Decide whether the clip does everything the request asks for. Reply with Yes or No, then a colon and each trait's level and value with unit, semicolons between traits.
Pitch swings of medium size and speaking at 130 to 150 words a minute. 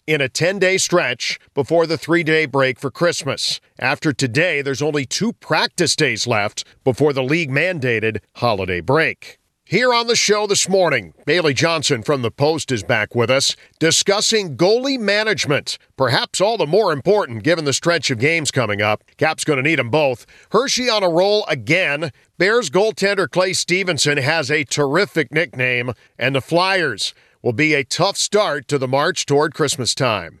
No: average, 4.7 semitones; average, 175 wpm